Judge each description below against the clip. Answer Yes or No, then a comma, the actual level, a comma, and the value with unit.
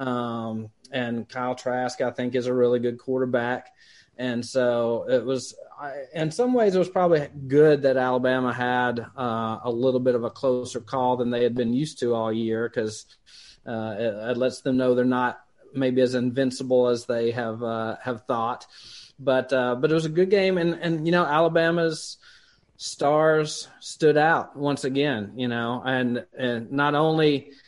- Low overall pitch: Yes, low, 125 Hz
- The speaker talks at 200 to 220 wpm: No, average, 180 wpm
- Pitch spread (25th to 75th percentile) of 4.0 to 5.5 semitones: No, average, 3.1 semitones